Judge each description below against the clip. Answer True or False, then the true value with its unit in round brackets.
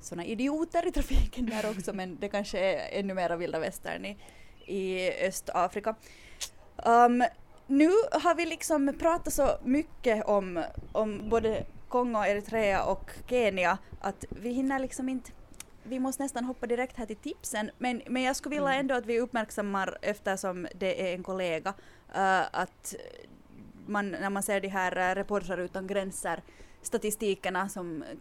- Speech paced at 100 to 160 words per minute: True (155 wpm)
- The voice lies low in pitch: False (215 Hz)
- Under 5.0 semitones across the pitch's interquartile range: False (5.3 semitones)